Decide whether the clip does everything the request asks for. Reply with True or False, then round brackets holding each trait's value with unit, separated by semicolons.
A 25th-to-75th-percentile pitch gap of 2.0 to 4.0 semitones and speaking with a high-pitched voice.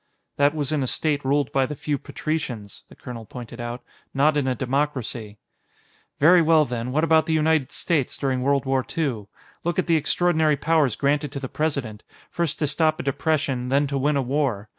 False (3.3 semitones; 140 Hz)